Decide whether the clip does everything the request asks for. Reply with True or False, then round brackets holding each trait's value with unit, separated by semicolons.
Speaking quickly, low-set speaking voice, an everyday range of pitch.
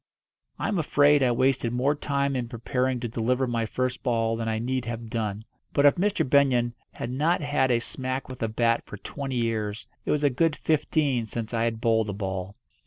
True (210 wpm; 125 Hz; 3.4 semitones)